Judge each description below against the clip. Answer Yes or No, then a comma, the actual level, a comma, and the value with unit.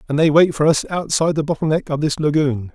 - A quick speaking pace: Yes, fast, 260 wpm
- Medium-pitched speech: Yes, medium, 150 Hz